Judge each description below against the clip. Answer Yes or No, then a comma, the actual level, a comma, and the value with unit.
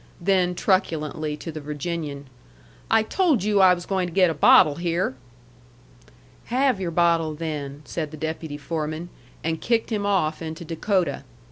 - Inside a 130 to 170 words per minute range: Yes, average, 155 wpm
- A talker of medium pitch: Yes, medium, 165 Hz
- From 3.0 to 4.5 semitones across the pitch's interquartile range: Yes, average, 3.4 semitones